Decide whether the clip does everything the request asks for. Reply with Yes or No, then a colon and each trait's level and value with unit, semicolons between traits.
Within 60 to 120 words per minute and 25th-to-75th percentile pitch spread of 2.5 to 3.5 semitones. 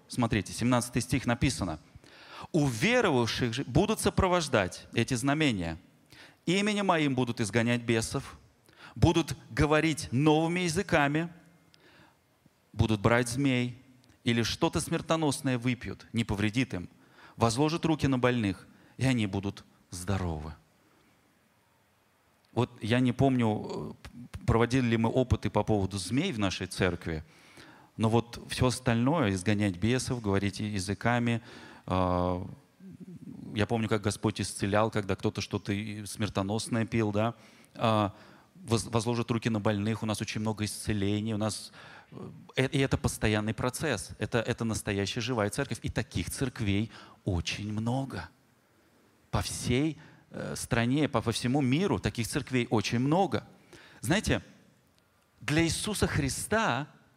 No: average, 115 wpm; average, 4.1 semitones